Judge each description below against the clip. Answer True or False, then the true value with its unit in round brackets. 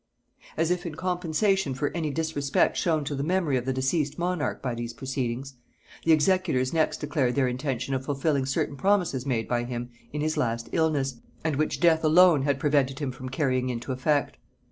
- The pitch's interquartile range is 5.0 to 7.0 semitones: False (3.6 semitones)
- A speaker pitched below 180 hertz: True (140 Hz)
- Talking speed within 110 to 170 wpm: False (190 wpm)